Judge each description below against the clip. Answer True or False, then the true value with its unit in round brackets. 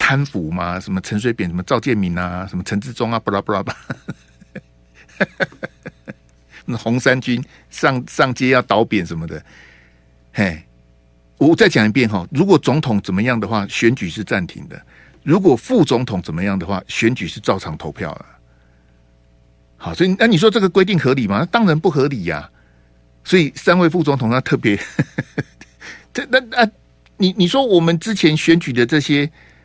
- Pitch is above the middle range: False (115 Hz)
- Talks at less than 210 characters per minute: False (255 characters per minute)